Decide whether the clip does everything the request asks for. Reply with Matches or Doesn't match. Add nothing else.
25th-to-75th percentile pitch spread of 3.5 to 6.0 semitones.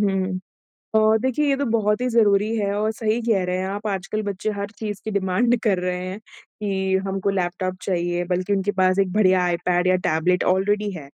Doesn't match